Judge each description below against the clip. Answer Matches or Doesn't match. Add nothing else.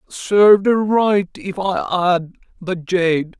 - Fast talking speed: Doesn't match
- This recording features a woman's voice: Doesn't match